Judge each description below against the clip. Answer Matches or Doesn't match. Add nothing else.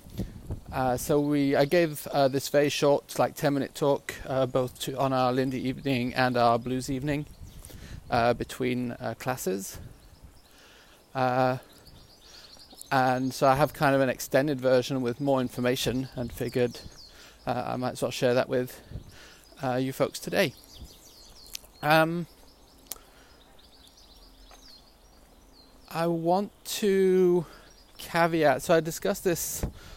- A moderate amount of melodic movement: Matches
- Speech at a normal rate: Doesn't match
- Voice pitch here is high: Doesn't match